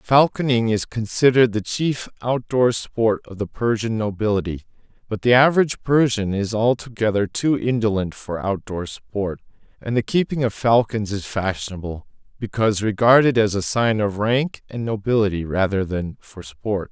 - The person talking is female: No, male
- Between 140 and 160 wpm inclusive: Yes, average, 155 wpm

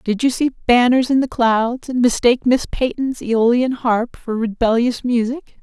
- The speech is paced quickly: No, average, 170 wpm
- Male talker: No, female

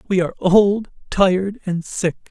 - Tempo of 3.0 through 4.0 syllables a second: No, 4.6 syllables/s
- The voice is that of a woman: No, male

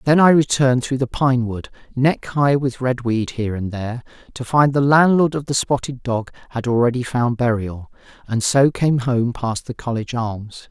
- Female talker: No, male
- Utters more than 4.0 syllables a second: Yes, 4.9 syllables/s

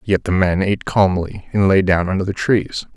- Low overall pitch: Yes, very low, 95 Hz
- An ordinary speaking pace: No, fast, 225 wpm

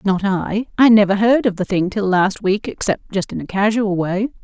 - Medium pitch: No, high, 205 Hz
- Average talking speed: No, fast, 230 wpm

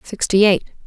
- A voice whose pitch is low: No, high, 200 Hz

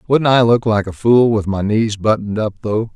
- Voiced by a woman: No, male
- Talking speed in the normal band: No, fast, 245 wpm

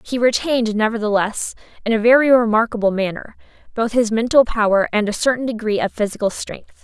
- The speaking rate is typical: Yes, average, 165 wpm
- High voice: Yes, high, 225 Hz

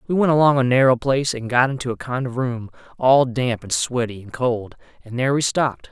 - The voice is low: Yes, low, 125 Hz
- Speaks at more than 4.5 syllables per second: Yes, 5.7 syllables/s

